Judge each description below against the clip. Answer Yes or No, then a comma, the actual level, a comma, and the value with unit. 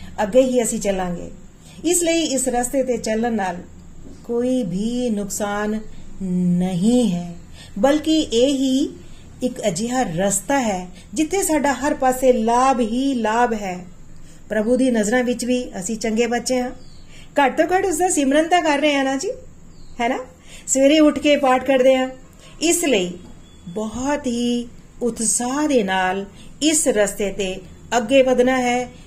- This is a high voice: Yes, high, 245 Hz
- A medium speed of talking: Yes, average, 120 wpm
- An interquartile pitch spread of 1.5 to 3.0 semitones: No, average, 4.4 semitones